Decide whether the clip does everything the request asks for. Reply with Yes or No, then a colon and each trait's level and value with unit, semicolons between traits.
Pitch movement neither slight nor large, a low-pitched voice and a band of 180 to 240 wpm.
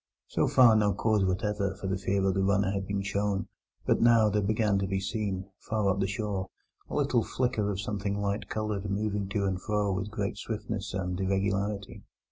No: narrow, 1.4 semitones; low, 100 Hz; average, 200 wpm